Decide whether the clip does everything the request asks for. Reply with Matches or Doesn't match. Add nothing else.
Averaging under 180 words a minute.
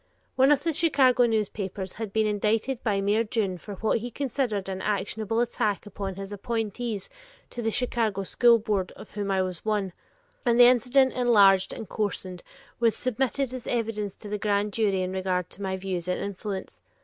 Doesn't match